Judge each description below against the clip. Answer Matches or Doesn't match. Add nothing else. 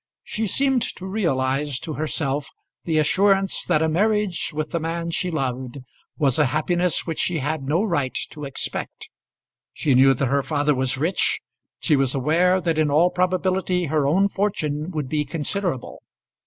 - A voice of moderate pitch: Matches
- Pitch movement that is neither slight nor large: Matches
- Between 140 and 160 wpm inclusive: Doesn't match